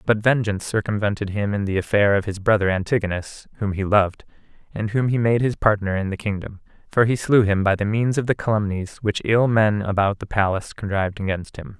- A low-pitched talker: Yes, low, 105 Hz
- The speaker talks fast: Yes, fast, 215 wpm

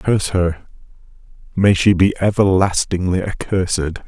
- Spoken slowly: Yes, slow, 105 wpm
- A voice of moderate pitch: No, very low, 95 Hz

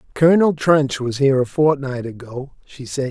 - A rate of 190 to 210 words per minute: No, average, 175 wpm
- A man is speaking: Yes, male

